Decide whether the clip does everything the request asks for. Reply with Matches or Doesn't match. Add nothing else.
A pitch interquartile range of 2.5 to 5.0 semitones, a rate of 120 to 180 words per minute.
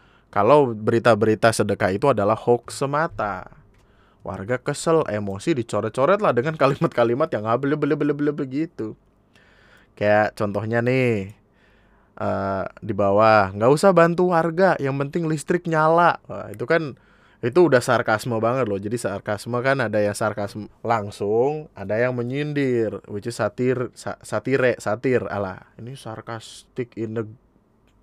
Doesn't match